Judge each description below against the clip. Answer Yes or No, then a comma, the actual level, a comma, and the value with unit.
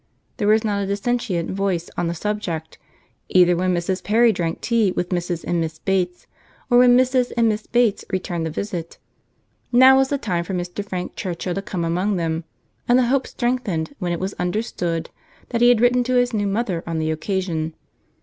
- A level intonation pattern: No, average, 5.2 semitones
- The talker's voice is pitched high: Yes, high, 195 Hz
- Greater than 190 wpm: Yes, average, 200 wpm